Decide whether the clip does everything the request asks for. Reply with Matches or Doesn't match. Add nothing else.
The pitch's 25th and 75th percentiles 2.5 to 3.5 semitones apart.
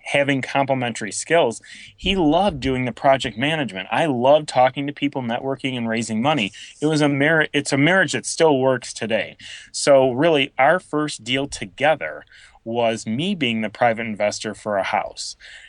Doesn't match